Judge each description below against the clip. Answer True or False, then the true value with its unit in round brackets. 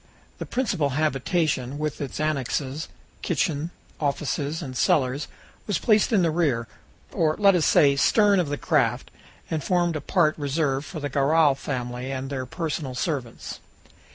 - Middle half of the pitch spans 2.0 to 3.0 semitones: False (3.4 semitones)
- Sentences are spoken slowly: False (155 wpm)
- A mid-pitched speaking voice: True (150 Hz)